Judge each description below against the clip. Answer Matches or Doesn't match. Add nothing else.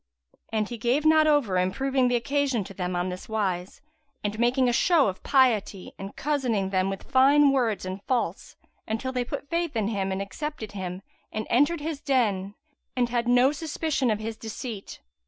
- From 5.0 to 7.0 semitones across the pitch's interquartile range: Matches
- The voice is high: Matches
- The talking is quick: Doesn't match